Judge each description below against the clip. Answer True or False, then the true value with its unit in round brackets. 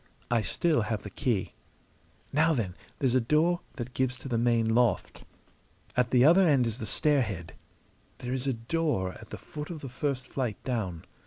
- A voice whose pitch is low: True (125 Hz)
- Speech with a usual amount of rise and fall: True (4.3 semitones)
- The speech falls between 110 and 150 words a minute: False (185 wpm)